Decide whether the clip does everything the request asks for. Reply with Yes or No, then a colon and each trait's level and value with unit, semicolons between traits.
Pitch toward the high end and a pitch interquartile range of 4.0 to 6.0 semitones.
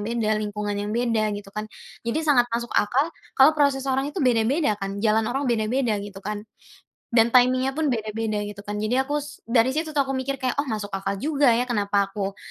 Yes: high, 235 Hz; average, 4.3 semitones